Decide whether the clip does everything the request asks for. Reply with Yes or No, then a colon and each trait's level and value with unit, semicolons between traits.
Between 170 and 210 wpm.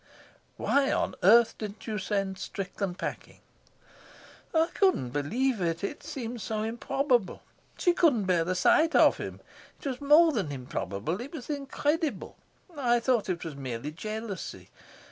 No: average, 145 wpm